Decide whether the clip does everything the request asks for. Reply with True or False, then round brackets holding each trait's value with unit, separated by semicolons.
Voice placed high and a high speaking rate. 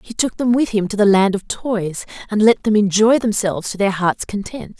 True (205 Hz; 240 wpm)